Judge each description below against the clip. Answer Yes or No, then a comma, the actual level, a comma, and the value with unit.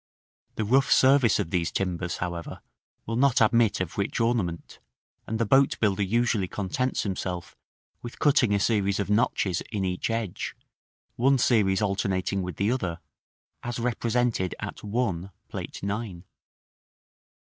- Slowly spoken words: No, average, 145 wpm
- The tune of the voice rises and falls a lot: No, average, 4.2 semitones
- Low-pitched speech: Yes, low, 105 Hz